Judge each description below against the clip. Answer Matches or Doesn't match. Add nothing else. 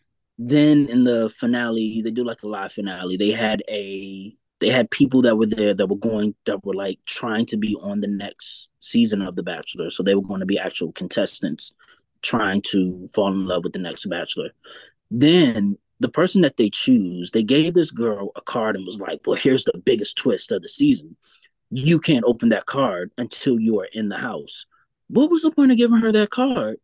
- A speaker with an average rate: Doesn't match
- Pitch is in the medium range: Doesn't match